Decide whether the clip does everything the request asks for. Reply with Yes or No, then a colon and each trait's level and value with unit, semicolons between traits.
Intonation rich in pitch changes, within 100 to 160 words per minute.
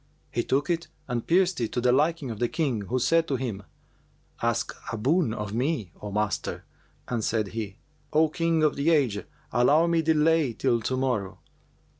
No: wide, 5.8 semitones; average, 185 wpm